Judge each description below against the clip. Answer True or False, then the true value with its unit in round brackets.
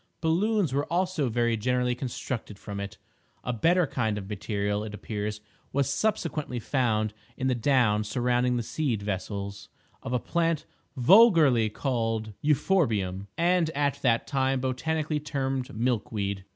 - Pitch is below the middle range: True (125 Hz)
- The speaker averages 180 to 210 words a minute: False (140 wpm)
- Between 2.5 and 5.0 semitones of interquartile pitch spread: False (5.5 semitones)